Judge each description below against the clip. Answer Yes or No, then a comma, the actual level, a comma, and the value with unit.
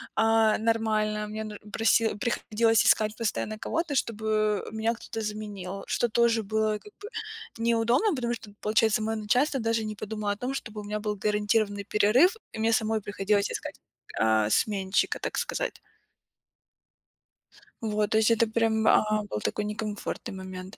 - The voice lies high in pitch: Yes, high, 215 Hz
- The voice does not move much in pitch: Yes, narrow, 1.4 semitones